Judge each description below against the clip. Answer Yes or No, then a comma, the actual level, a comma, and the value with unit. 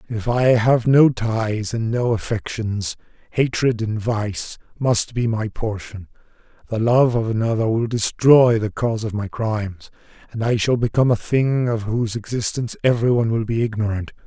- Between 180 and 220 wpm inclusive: No, average, 165 wpm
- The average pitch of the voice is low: Yes, low, 115 Hz